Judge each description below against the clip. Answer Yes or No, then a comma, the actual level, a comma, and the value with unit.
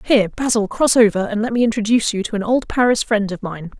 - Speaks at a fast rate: Yes, fast, 255 wpm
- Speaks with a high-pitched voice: Yes, high, 220 Hz